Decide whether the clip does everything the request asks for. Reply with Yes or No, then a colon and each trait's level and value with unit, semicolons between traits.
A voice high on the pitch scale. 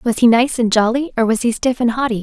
Yes: high, 235 Hz